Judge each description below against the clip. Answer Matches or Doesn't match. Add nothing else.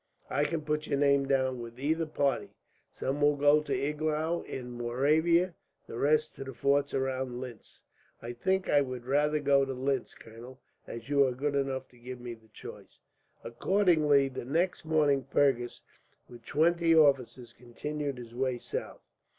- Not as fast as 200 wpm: Matches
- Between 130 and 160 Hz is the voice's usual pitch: Matches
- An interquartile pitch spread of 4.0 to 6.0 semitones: Doesn't match